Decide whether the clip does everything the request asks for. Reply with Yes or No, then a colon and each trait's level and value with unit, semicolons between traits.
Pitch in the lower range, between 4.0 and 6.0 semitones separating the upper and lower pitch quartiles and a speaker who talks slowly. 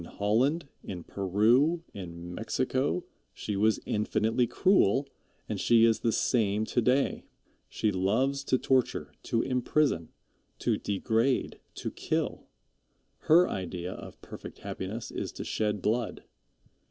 Yes: low, 115 Hz; average, 4.6 semitones; slow, 130 wpm